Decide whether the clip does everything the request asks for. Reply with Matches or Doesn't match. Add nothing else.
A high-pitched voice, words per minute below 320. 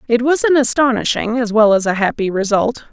Matches